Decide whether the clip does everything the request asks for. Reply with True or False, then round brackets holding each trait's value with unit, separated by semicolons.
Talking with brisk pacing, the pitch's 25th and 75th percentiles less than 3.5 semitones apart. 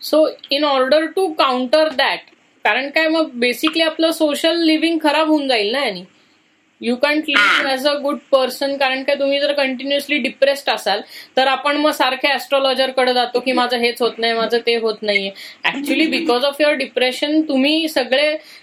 True (170 wpm; 3.0 semitones)